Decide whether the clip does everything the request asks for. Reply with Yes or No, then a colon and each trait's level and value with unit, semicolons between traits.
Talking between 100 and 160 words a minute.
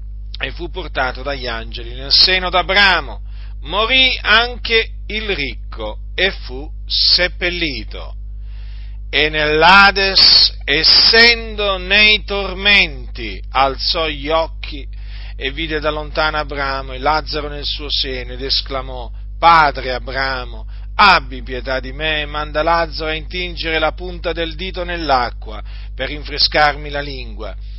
Yes: average, 120 wpm